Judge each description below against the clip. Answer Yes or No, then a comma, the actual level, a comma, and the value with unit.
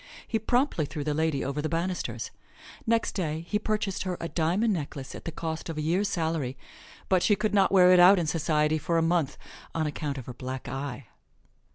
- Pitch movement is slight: No, average, 3.8 semitones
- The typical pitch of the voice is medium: Yes, medium, 165 Hz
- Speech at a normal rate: No, fast, 210 wpm